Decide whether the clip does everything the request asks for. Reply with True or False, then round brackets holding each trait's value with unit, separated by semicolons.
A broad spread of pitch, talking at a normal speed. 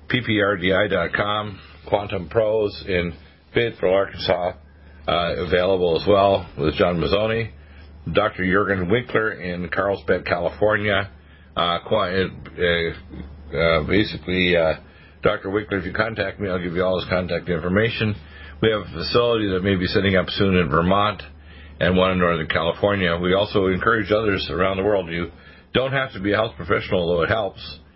False (3.4 semitones; 150 wpm)